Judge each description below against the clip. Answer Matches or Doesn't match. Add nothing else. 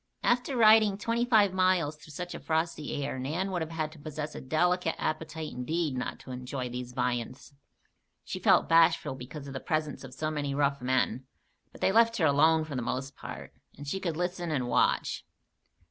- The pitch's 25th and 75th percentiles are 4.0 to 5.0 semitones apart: Matches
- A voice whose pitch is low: Doesn't match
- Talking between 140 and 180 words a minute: Doesn't match